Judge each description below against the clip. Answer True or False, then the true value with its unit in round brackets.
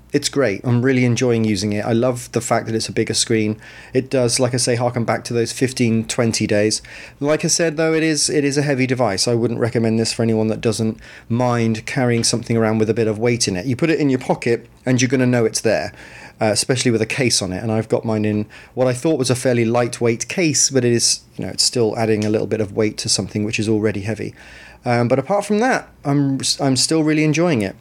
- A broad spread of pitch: False (2.8 semitones)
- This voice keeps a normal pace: False (260 wpm)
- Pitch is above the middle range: False (120 Hz)